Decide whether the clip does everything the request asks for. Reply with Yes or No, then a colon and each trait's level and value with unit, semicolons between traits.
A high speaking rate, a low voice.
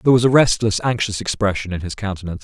Yes: fast, 220 wpm; low, 105 Hz